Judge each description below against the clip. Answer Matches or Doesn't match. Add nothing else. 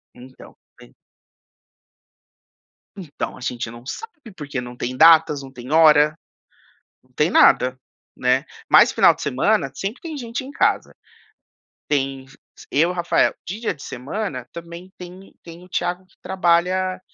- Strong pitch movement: Matches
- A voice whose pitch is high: Doesn't match